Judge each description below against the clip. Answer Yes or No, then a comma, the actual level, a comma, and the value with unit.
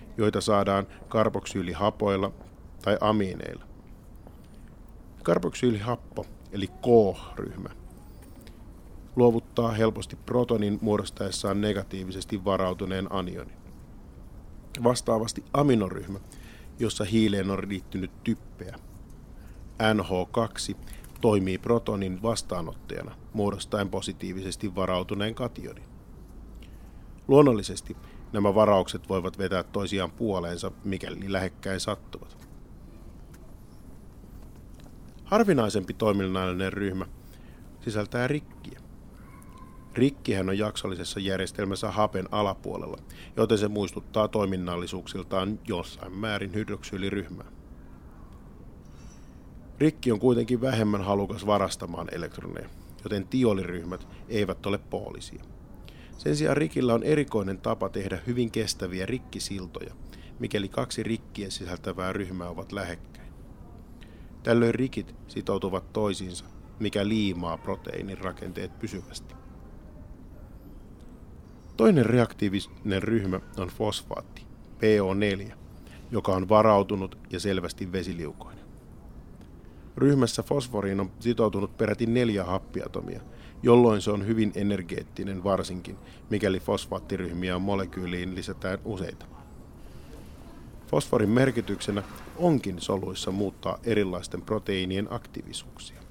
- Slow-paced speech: Yes, slow, 85 wpm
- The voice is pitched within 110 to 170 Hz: No, low, 100 Hz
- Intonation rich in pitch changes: No, average, 2.9 semitones